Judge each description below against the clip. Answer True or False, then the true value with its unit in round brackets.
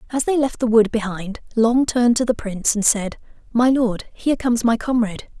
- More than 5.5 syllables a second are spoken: True (5.7 syllables/s)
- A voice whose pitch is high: True (230 Hz)